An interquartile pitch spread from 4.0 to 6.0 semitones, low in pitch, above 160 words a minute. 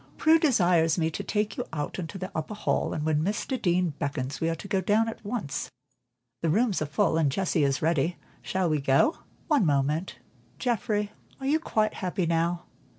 No: average, 5.0 semitones; medium, 175 Hz; average, 195 wpm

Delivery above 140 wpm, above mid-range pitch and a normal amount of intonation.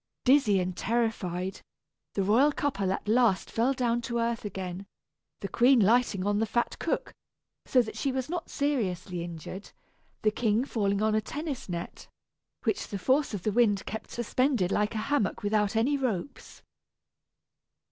Yes: average, 160 wpm; high, 220 Hz; average, 4.2 semitones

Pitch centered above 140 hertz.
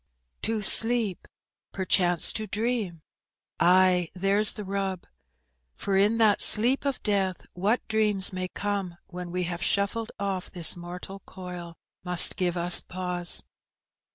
Yes: high, 190 Hz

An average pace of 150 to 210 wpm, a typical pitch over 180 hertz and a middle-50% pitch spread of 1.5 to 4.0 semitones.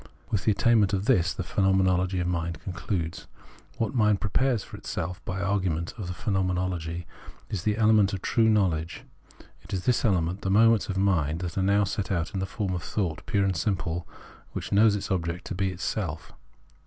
No: average, 190 wpm; very low, 95 Hz; average, 2.8 semitones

